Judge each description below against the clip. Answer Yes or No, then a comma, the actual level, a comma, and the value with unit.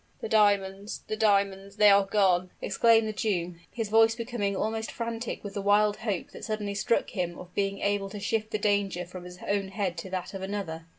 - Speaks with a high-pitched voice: Yes, high, 200 Hz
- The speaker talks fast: Yes, fast, 210 wpm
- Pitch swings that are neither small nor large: No, narrow, 2.0 semitones